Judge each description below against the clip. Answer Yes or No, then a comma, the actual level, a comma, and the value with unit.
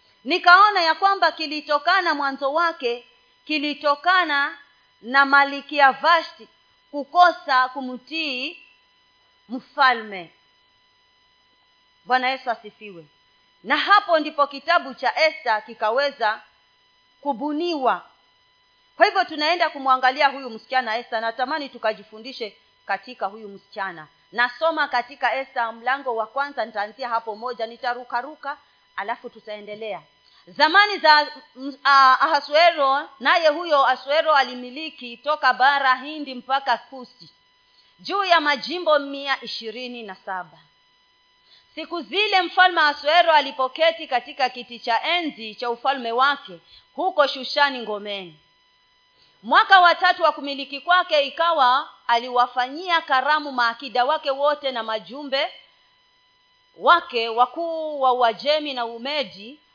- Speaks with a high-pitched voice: Yes, very high, 275 Hz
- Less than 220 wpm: Yes, average, 105 wpm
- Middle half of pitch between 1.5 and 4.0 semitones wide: No, average, 5.0 semitones